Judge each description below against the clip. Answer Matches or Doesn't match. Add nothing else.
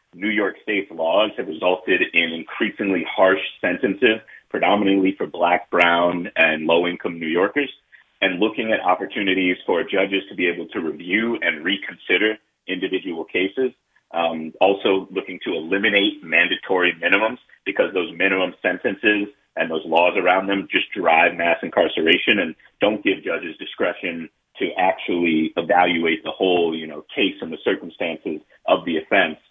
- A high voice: Doesn't match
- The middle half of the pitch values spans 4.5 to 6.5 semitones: Doesn't match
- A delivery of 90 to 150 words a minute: Matches